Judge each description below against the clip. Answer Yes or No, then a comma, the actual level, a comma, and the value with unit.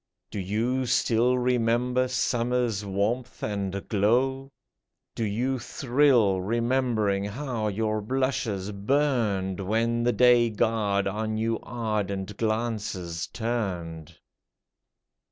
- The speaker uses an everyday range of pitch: Yes, average, 3.5 semitones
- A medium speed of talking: No, slow, 100 wpm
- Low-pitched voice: Yes, low, 115 Hz